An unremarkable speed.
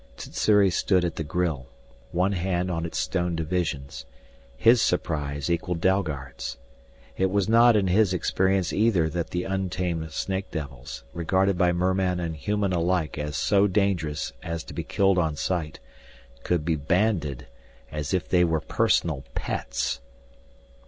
Yes: average, 145 wpm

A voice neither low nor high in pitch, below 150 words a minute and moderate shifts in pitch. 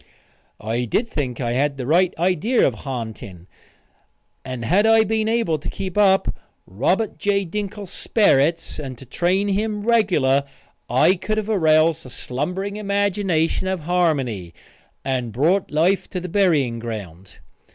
No: medium, 165 Hz; average, 140 wpm; wide, 7.4 semitones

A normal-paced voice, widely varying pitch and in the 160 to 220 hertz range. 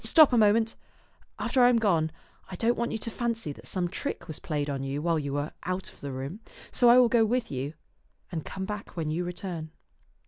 No: fast, 230 wpm; wide, 6.7 semitones; medium, 185 Hz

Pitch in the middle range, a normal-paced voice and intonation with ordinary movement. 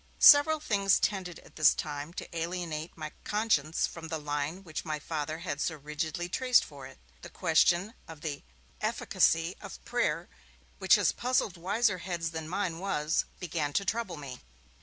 Yes: medium, 165 Hz; average, 165 wpm; average, 4.0 semitones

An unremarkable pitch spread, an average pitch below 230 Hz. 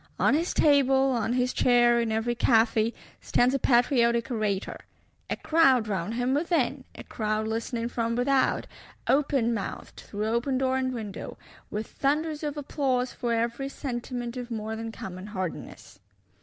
No: average, 3.1 semitones; high, 240 Hz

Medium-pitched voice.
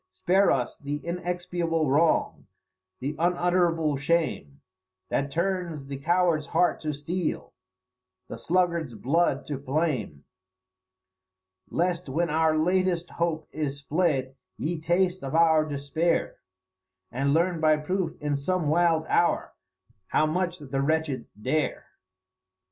Yes: medium, 160 Hz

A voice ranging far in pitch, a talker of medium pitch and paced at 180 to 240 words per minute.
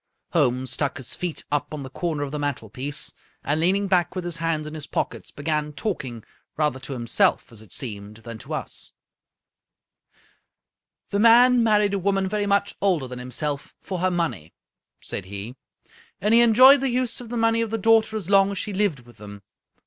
Yes: wide, 7.6 semitones; medium, 165 Hz; average, 200 wpm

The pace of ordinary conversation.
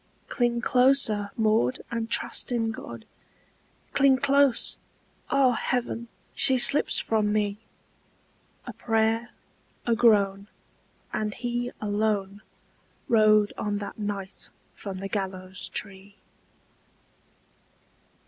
No: slow, 100 wpm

